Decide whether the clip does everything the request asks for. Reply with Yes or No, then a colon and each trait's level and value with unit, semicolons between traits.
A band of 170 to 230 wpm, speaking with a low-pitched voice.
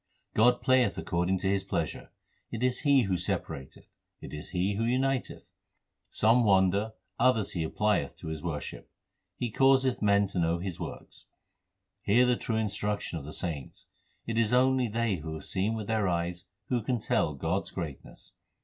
Yes: average, 175 wpm; low, 100 Hz